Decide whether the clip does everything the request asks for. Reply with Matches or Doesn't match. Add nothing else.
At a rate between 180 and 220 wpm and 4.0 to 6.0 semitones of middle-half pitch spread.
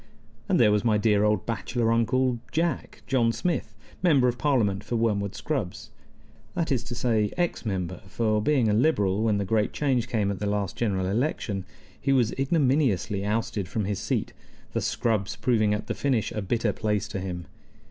Doesn't match